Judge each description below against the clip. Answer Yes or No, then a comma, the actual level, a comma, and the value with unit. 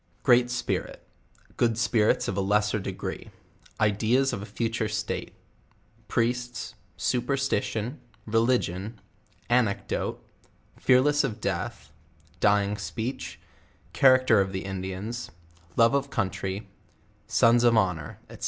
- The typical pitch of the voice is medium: No, low, 115 Hz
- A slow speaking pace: Yes, slow, 105 wpm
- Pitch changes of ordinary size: Yes, average, 3.3 semitones